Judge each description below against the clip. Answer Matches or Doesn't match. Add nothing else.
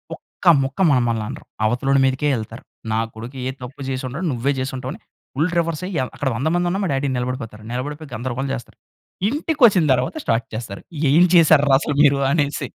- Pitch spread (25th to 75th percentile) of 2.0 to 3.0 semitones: Doesn't match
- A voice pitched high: Doesn't match